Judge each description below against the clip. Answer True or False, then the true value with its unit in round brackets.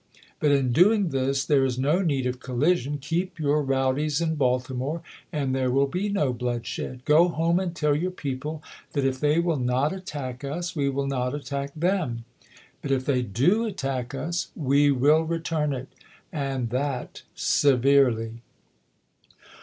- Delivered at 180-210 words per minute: False (160 wpm)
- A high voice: False (140 Hz)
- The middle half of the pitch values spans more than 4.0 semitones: False (3.5 semitones)